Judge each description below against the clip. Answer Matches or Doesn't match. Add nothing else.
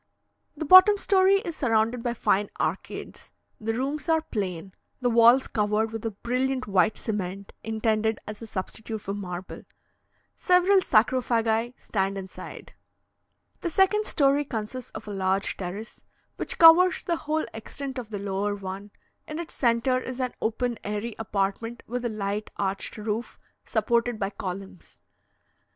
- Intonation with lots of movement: Doesn't match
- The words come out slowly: Doesn't match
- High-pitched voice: Matches